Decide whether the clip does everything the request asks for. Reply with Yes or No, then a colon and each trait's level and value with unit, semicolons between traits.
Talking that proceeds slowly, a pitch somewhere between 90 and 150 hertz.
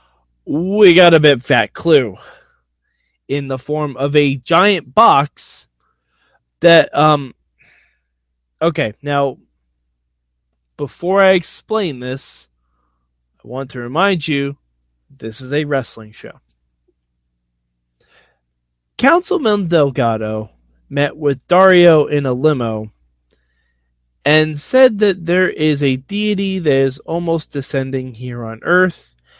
Yes: slow, 110 wpm; low, 135 Hz